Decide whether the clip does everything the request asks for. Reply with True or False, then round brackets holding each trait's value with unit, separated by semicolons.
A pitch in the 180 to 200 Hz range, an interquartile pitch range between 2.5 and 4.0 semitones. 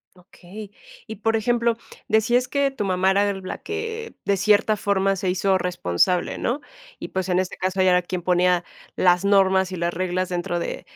True (190 Hz; 2.9 semitones)